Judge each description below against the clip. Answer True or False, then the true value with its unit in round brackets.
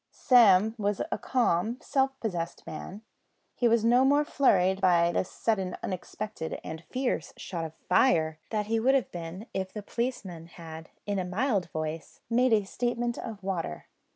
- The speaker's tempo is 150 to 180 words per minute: True (165 wpm)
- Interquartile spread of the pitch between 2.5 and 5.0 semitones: False (5.5 semitones)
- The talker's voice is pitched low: False (200 Hz)